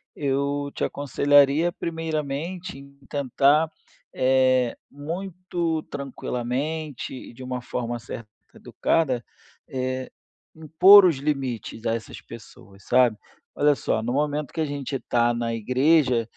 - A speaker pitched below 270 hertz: Yes, medium, 140 Hz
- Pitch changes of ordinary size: Yes, average, 3.7 semitones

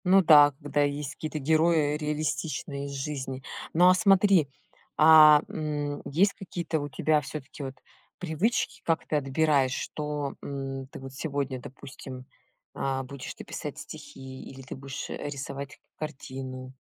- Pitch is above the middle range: No, medium, 145 Hz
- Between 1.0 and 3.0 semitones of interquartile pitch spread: Yes, narrow, 2.6 semitones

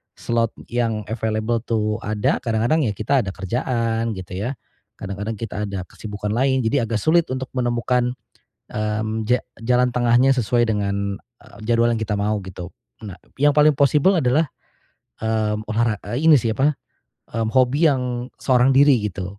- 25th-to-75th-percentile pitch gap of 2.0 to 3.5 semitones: Yes, average, 2.9 semitones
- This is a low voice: Yes, low, 115 Hz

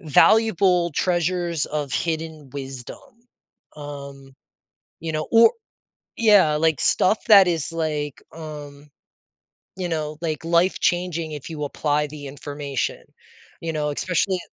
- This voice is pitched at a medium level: Yes, medium, 155 Hz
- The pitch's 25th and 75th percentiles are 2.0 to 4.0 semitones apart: Yes, average, 3.2 semitones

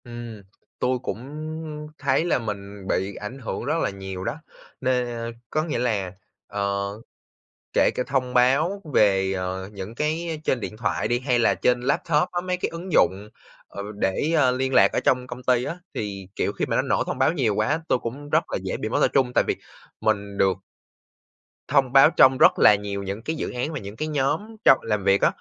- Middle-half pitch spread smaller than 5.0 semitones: No, wide, 5.6 semitones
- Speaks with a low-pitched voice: Yes, low, 125 Hz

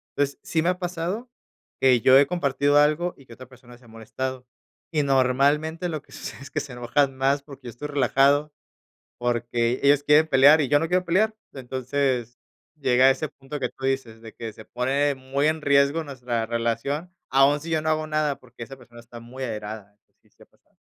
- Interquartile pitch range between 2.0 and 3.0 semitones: No, average, 3.4 semitones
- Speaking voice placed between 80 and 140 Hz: Yes, low, 135 Hz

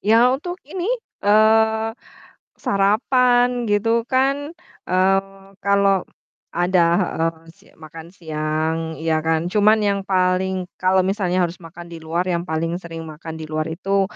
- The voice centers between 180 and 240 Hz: Yes, high, 190 Hz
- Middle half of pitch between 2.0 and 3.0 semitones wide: No, average, 4.7 semitones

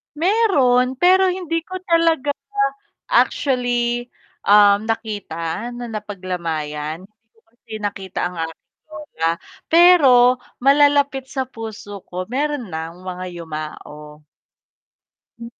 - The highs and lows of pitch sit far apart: Yes, wide, 7.9 semitones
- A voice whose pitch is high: Yes, high, 225 Hz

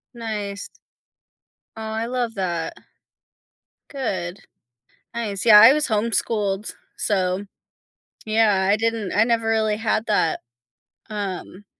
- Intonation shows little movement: Yes, narrow, 2.3 semitones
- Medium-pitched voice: No, high, 215 Hz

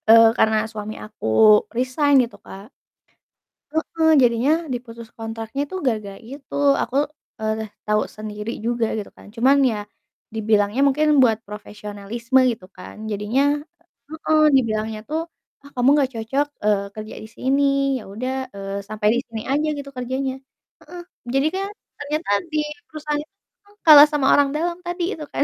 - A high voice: Yes, high, 235 Hz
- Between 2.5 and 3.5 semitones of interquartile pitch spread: No, average, 4.7 semitones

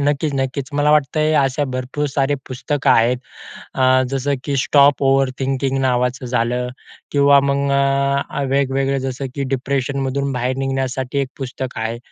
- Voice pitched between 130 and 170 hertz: Yes, low, 135 Hz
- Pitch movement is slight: Yes, narrow, 1.4 semitones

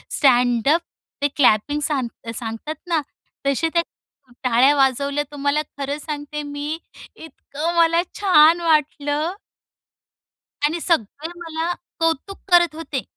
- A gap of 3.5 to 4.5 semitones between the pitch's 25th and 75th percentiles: No, average, 2.8 semitones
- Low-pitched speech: No, very high, 295 Hz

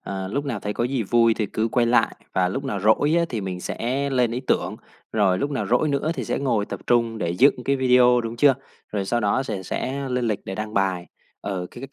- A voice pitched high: No, low, 115 Hz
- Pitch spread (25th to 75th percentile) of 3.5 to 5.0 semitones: Yes, average, 4.4 semitones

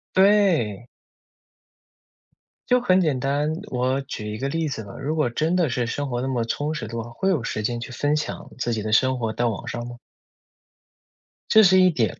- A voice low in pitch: Yes, low, 130 Hz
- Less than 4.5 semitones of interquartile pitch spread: No, average, 4.9 semitones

